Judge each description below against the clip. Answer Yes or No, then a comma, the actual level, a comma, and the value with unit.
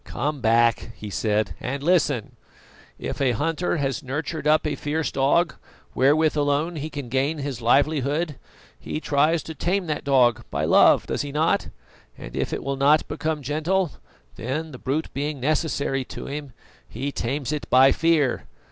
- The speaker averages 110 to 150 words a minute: No, average, 165 wpm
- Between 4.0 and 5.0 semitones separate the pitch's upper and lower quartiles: No, average, 2.7 semitones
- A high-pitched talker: No, medium, 145 Hz